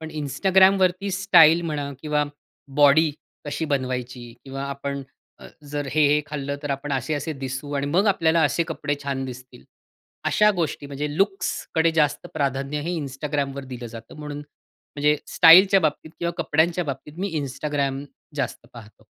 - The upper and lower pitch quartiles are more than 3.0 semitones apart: No, average, 2.7 semitones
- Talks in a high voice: No, medium, 145 Hz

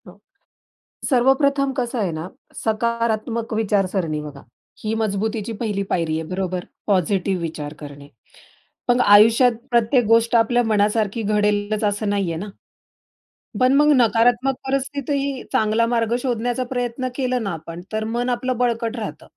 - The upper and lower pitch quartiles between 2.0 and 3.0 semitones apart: No, average, 3.5 semitones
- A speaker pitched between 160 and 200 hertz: No, high, 225 Hz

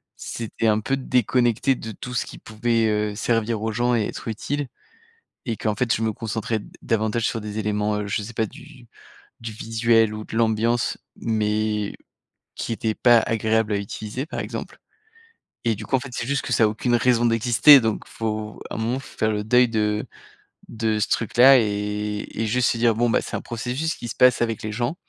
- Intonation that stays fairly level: Yes, narrow, 2.0 semitones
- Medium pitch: No, low, 115 Hz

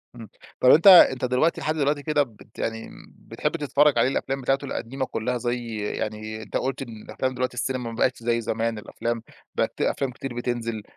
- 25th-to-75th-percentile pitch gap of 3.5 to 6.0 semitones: No, average, 2.9 semitones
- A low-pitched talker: Yes, low, 125 Hz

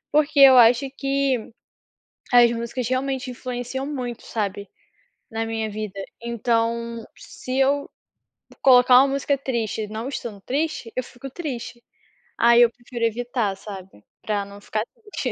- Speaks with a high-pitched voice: Yes, high, 240 Hz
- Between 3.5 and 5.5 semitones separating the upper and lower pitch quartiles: No, average, 2.8 semitones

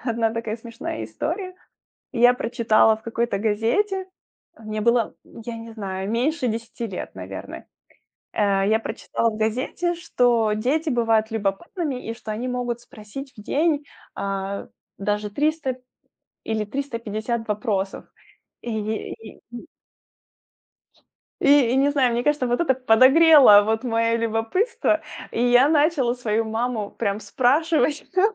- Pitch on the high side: Yes, high, 230 Hz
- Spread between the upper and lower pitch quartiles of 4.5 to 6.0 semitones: No, average, 3.5 semitones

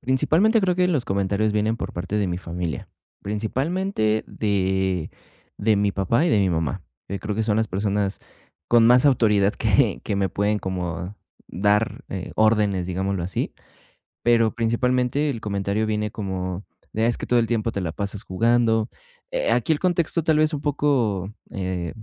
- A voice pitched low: Yes, low, 105 Hz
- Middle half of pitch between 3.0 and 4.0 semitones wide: Yes, average, 3.7 semitones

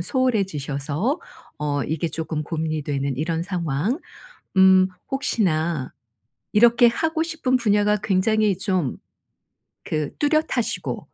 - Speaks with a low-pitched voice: No, medium, 185 Hz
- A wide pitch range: Yes, wide, 7.2 semitones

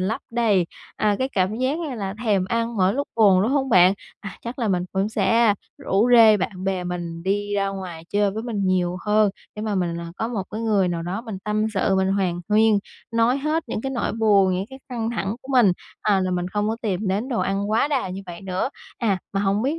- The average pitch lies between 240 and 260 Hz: No, high, 205 Hz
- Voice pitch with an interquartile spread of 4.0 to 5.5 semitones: No, average, 3.3 semitones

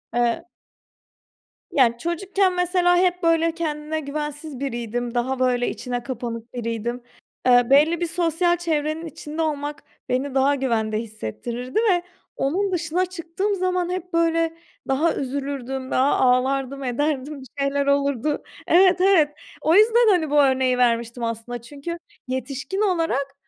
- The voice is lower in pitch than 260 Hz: No, very high, 285 Hz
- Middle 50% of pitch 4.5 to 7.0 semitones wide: Yes, average, 5.1 semitones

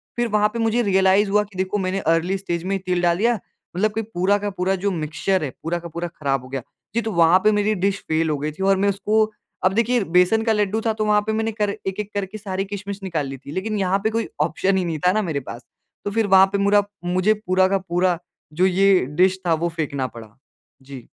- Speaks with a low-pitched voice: No, high, 190 Hz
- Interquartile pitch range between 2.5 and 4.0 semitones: Yes, average, 3.3 semitones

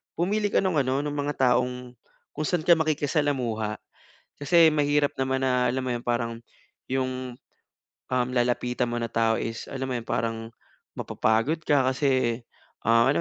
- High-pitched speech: No, low, 130 Hz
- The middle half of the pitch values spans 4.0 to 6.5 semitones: No, average, 3.4 semitones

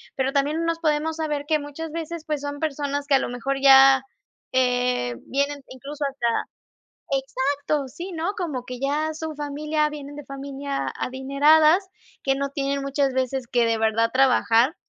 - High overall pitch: Yes, very high, 280 Hz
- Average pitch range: No, narrow, 2.2 semitones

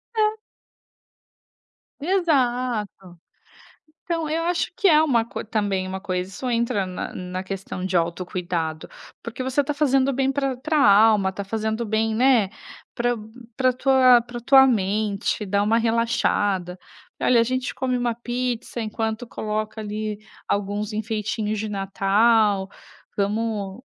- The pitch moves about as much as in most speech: Yes, average, 3.9 semitones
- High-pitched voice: Yes, high, 225 Hz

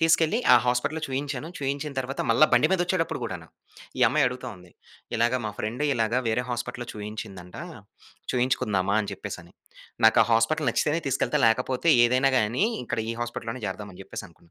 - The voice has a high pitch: No, low, 125 Hz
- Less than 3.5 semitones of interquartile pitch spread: No, average, 4.0 semitones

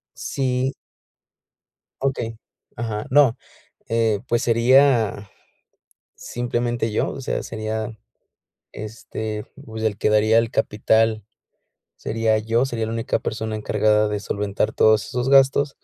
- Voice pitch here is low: Yes, low, 110 Hz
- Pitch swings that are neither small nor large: No, narrow, 1.9 semitones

